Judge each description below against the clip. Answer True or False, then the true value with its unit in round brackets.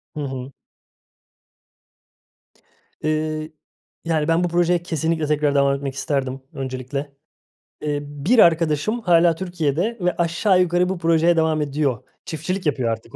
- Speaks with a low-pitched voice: False (155 Hz)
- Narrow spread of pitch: False (3.4 semitones)